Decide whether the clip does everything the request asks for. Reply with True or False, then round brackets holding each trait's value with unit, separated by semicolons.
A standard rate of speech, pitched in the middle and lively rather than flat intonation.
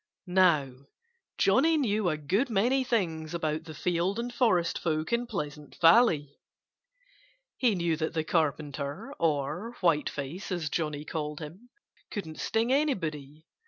False (130 wpm; 170 Hz; 5.9 semitones)